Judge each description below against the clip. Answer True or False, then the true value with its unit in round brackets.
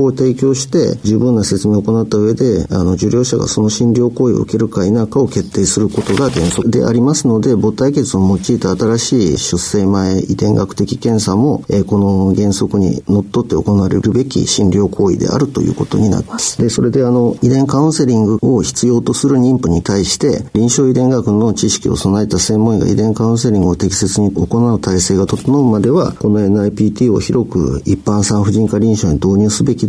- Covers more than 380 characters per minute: True (390 characters per minute)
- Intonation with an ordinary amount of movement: True (3.6 semitones)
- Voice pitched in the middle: False (110 Hz)